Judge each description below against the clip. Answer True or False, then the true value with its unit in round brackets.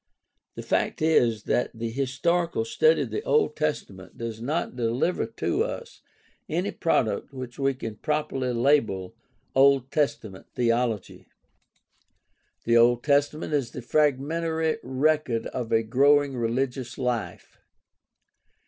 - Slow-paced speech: True (120 wpm)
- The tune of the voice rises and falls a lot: False (4.3 semitones)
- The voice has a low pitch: True (130 Hz)